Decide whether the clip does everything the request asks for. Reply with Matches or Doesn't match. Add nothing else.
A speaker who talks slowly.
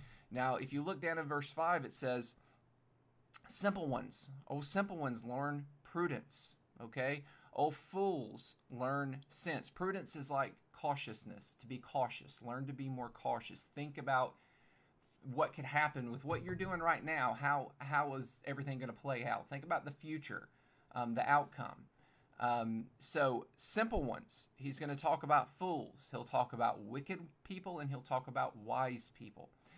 Doesn't match